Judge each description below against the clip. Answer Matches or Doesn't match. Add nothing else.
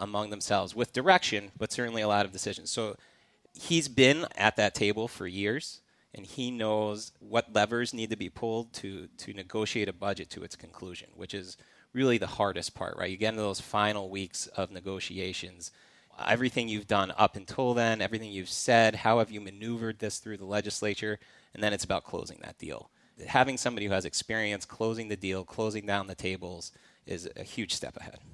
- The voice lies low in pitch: Matches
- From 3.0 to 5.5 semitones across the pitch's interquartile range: Doesn't match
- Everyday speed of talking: Matches